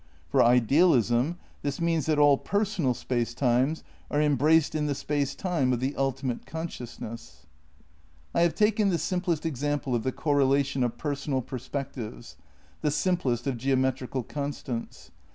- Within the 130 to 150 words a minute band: Yes, average, 145 wpm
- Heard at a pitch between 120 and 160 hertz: Yes, medium, 140 Hz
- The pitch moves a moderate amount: Yes, average, 3.7 semitones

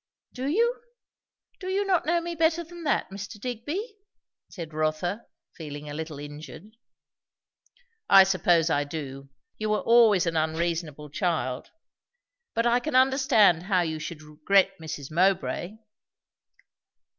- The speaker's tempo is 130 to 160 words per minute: Yes, slow, 135 wpm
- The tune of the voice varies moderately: No, wide, 8.4 semitones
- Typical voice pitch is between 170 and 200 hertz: Yes, medium, 185 Hz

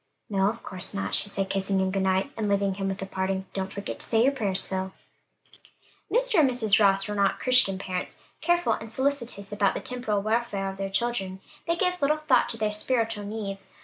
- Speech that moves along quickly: Yes, fast, 215 wpm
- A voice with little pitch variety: No, average, 3.7 semitones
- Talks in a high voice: Yes, high, 200 Hz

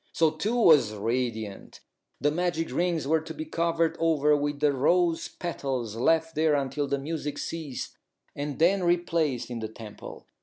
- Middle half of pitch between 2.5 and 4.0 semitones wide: Yes, average, 3.5 semitones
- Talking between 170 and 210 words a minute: No, average, 160 wpm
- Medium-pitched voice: Yes, medium, 150 Hz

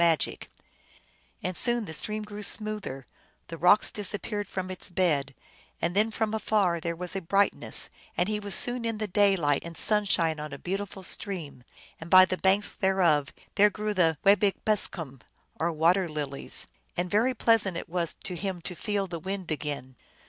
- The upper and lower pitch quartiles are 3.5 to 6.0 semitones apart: Yes, average, 3.8 semitones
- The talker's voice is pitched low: No, medium, 185 Hz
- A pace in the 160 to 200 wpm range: Yes, average, 180 wpm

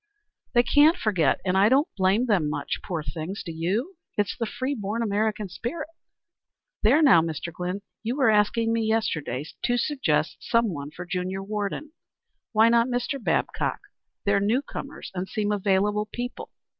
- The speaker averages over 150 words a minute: Yes, average, 165 wpm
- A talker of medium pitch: No, high, 210 Hz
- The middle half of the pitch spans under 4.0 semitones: No, average, 4.3 semitones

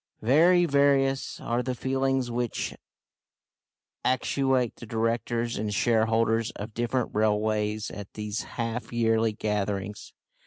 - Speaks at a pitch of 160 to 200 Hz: No, low, 115 Hz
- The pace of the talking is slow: Yes, slow, 110 wpm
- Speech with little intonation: No, average, 3.1 semitones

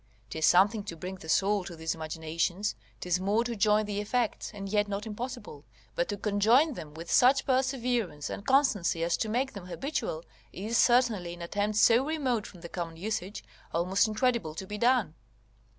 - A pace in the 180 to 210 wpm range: Yes, average, 185 wpm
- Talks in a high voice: Yes, high, 205 Hz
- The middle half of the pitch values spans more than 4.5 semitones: Yes, average, 5.3 semitones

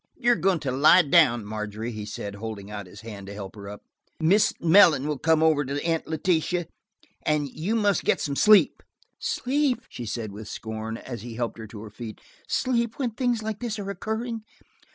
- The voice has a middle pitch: Yes, medium, 145 Hz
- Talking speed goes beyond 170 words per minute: Yes, average, 200 wpm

